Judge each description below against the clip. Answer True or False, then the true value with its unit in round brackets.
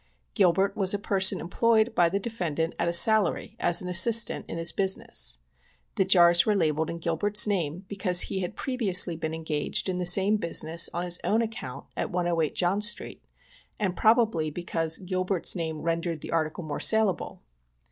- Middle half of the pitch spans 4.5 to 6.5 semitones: False (3.4 semitones)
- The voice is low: False (180 Hz)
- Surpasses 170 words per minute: True (180 wpm)